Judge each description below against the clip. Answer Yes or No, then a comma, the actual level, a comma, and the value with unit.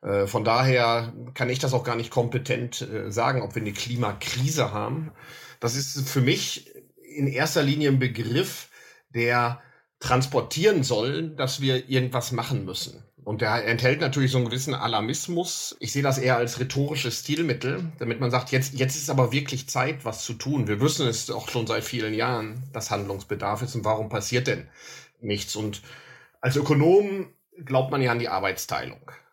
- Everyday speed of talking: Yes, average, 170 wpm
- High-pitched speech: No, low, 125 Hz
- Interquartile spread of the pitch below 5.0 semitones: Yes, narrow, 2.5 semitones